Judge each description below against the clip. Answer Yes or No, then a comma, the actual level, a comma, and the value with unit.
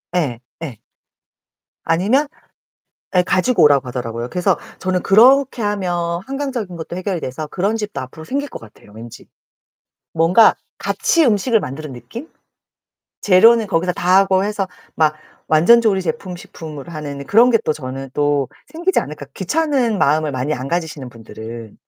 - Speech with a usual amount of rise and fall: No, wide, 6.8 semitones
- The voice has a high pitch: No, medium, 175 Hz